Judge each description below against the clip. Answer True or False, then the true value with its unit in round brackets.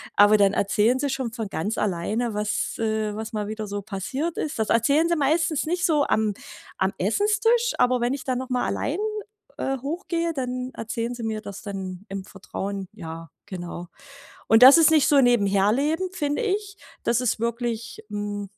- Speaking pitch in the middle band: False (235 Hz)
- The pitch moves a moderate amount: False (5.8 semitones)